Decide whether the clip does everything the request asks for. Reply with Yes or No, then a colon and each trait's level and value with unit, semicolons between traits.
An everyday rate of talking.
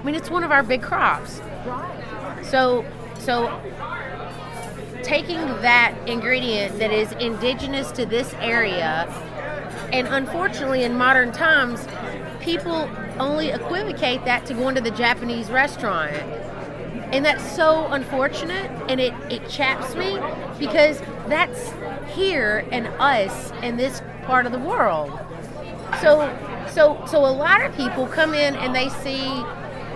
No: slow, 130 wpm